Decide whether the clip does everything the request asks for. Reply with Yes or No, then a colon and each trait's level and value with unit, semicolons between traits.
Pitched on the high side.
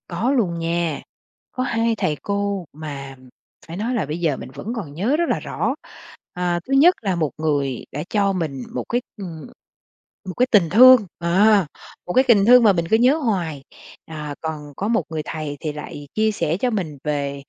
No: medium, 175 Hz